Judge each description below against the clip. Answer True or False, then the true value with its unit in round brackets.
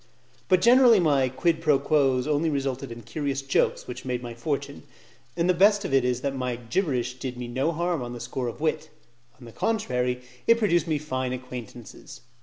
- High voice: False (135 Hz)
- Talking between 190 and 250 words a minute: True (200 wpm)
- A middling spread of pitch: True (4.5 semitones)